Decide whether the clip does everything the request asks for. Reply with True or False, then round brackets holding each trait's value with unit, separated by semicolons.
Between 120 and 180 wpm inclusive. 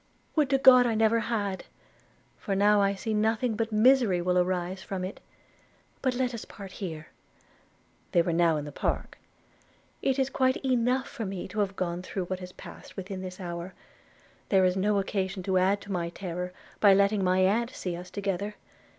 False (190 wpm)